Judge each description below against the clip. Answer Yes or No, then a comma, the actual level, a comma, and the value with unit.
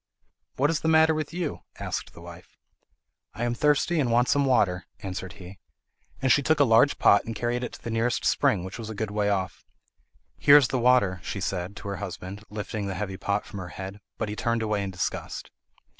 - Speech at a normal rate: No, fast, 220 wpm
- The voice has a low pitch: Yes, low, 110 Hz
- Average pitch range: Yes, average, 4.5 semitones